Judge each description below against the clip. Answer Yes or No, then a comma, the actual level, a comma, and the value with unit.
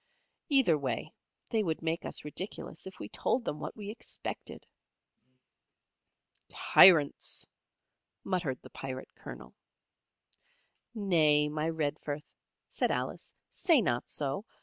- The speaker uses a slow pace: Yes, slow, 110 wpm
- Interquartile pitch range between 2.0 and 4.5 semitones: No, average, 5.1 semitones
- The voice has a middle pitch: Yes, medium, 155 Hz